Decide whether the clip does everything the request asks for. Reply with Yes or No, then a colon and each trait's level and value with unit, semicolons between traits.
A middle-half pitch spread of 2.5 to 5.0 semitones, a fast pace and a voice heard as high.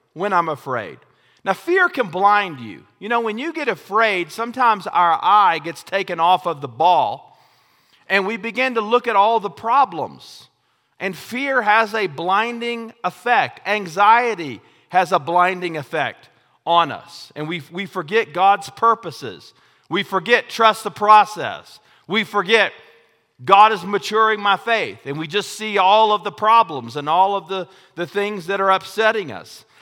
No: average, 3.7 semitones; average, 165 wpm; high, 200 Hz